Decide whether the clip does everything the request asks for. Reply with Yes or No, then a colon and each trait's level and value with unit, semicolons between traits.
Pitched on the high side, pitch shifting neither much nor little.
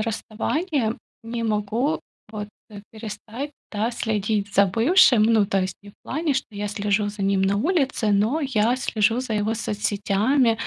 Yes: high, 220 Hz; average, 3.3 semitones